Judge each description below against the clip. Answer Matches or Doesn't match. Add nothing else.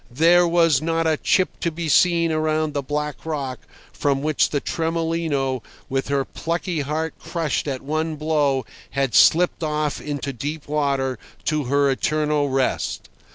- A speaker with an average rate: Matches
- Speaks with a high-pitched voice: Doesn't match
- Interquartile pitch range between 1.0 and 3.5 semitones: Matches